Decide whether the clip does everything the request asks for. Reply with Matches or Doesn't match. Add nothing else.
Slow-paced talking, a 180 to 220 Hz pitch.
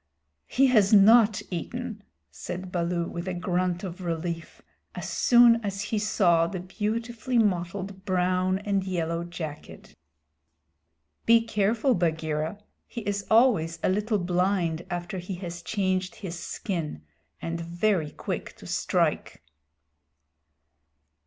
Matches